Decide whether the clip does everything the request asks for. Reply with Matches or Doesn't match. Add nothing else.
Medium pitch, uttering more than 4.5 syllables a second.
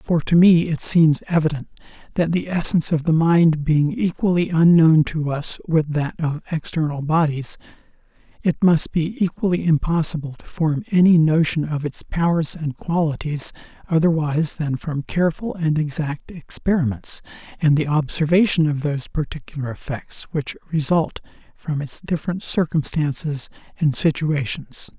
Matches